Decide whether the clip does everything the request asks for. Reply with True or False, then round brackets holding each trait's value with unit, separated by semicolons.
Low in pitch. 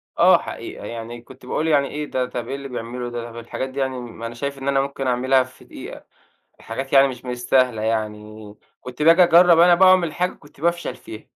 True (130 Hz)